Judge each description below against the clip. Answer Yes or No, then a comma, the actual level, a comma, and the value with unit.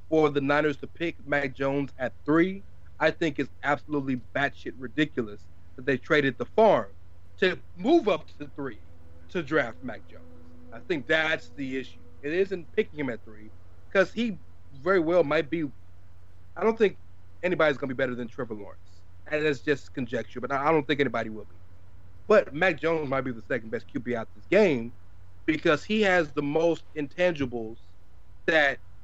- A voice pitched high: No, low, 135 Hz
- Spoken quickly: No, average, 180 wpm